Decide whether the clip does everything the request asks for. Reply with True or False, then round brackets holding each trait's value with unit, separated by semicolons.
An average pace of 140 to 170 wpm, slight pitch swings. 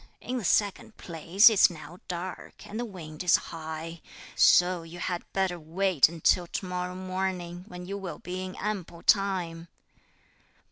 True (155 wpm; 2.2 semitones)